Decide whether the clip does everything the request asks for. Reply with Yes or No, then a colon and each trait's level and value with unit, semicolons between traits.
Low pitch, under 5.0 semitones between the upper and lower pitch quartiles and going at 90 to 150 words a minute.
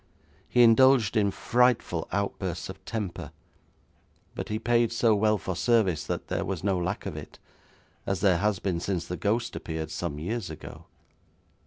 No: low, 100 Hz; average, 4.2 semitones; average, 165 wpm